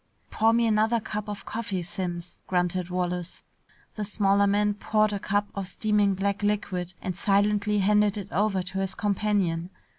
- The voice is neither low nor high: No, high, 200 Hz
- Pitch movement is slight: Yes, narrow, 2.2 semitones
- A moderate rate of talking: Yes, average, 160 wpm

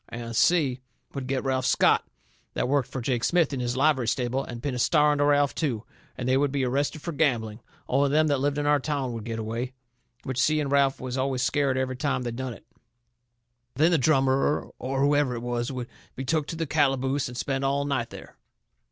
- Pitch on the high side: No, low, 135 Hz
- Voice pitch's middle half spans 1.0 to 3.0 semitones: Yes, narrow, 2.5 semitones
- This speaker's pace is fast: Yes, fast, 220 wpm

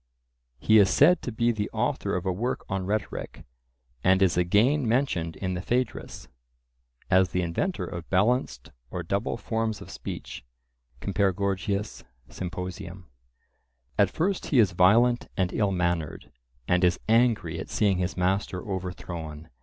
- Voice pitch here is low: Yes, very low, 95 Hz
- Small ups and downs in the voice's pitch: No, average, 3.8 semitones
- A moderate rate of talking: Yes, average, 145 wpm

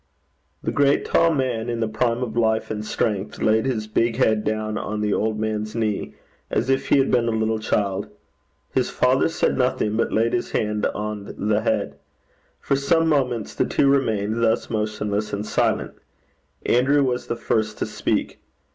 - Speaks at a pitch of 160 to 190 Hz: No, low, 110 Hz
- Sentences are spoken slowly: No, average, 180 wpm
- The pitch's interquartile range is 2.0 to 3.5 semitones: Yes, narrow, 2.5 semitones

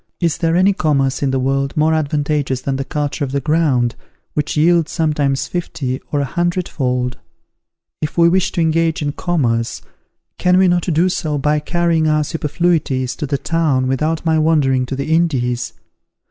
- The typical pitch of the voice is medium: Yes, medium, 150 Hz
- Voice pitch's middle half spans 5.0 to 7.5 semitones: No, average, 3.5 semitones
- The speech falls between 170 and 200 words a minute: Yes, average, 175 wpm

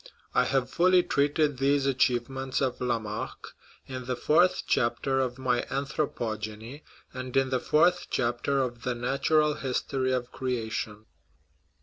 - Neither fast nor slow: No, slow, 130 wpm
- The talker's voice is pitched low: Yes, low, 130 Hz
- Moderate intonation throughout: No, narrow, 2.3 semitones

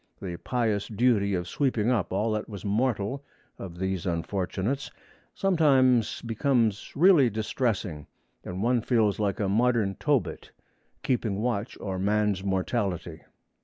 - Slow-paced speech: Yes, slow, 130 wpm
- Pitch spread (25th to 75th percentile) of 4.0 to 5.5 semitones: Yes, average, 4.3 semitones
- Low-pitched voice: Yes, low, 105 Hz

